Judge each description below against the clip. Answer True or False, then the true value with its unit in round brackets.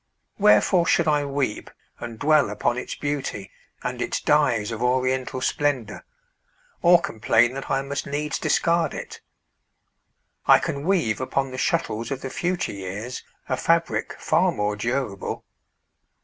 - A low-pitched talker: True (130 Hz)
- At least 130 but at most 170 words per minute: True (140 wpm)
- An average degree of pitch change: True (4.4 semitones)